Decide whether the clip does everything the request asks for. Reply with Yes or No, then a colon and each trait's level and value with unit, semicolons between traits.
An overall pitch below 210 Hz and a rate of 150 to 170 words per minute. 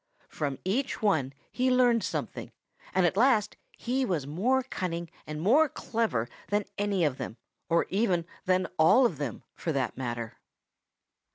Yes: medium, 185 Hz; average, 155 wpm